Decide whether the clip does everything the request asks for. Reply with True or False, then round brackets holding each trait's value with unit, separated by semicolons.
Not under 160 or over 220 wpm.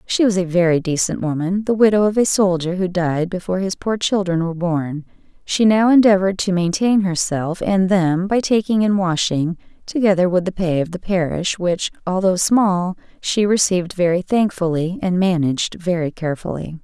True (175 wpm)